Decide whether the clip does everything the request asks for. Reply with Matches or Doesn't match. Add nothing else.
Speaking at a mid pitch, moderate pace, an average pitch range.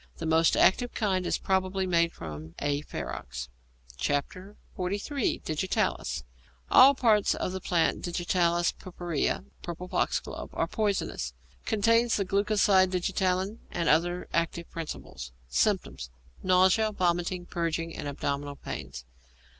Doesn't match